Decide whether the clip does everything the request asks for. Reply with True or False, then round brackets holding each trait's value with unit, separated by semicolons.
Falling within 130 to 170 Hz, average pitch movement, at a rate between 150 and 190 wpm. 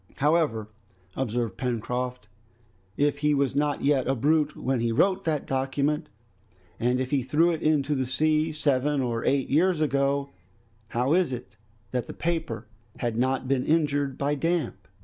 True (140 Hz; 3.2 semitones; 160 wpm)